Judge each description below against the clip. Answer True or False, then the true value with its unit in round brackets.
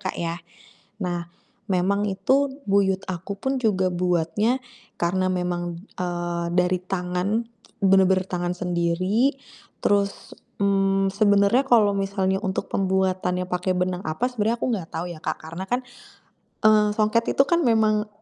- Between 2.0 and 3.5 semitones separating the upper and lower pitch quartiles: True (2.8 semitones)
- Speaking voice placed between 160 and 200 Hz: True (190 Hz)